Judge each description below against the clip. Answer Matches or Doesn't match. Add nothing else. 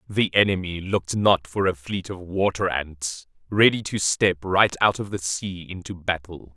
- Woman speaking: Doesn't match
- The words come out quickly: Doesn't match